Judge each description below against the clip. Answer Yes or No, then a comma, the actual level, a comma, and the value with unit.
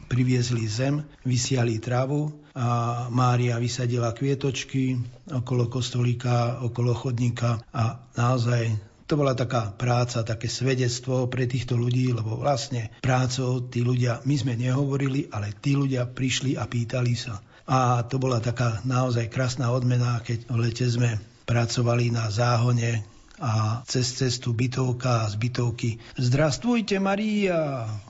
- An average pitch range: No, narrow, 1.6 semitones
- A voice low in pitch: Yes, low, 125 Hz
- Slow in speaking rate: No, average, 130 wpm